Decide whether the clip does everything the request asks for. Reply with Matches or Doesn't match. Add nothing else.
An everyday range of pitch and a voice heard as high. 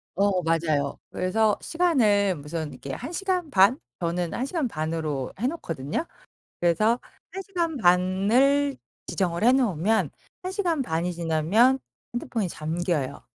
Doesn't match